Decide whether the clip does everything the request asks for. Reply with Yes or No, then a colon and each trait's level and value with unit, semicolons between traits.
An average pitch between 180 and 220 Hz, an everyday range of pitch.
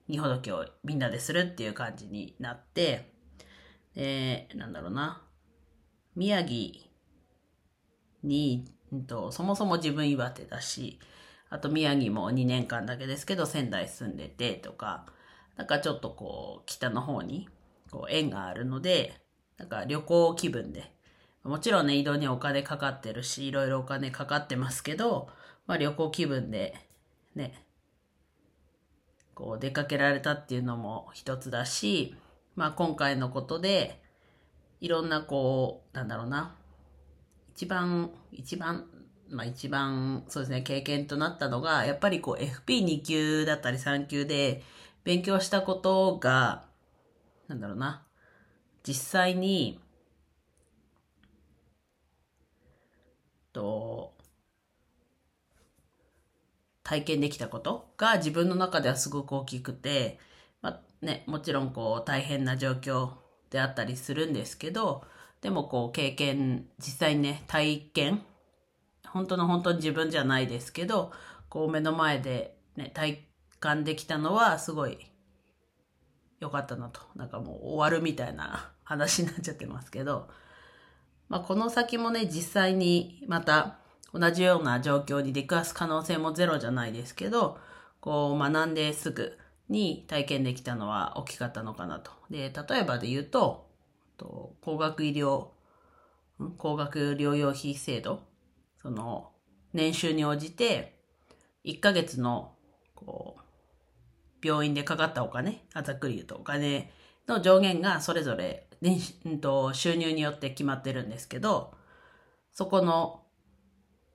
No: medium, 140 Hz; average, 4.9 semitones